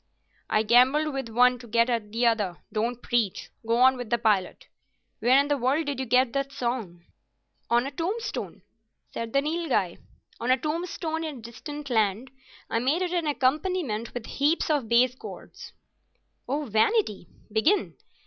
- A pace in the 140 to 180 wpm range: Yes, average, 165 wpm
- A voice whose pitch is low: No, very high, 250 Hz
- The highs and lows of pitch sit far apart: No, average, 4.3 semitones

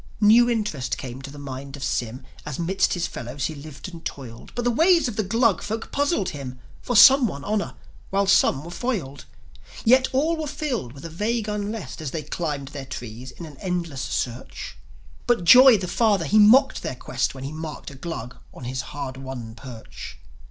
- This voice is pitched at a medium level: Yes, medium, 165 Hz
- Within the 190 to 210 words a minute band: Yes, average, 200 wpm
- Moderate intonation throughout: No, wide, 8.8 semitones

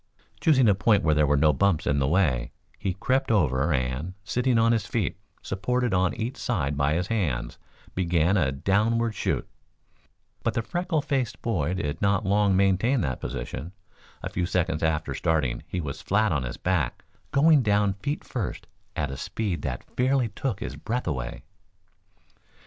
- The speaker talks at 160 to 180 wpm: Yes, average, 170 wpm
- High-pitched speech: No, very low, 95 Hz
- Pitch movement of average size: No, wide, 7.0 semitones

